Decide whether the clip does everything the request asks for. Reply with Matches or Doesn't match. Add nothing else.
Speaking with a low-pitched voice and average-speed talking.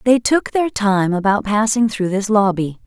Doesn't match